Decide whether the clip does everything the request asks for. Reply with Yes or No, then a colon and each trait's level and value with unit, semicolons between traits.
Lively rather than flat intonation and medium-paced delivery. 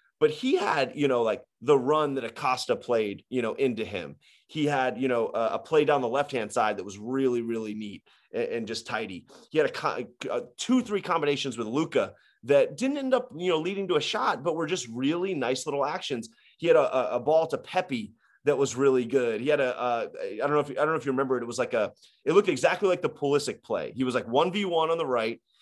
No: wide, 8.3 semitones; fast, 250 wpm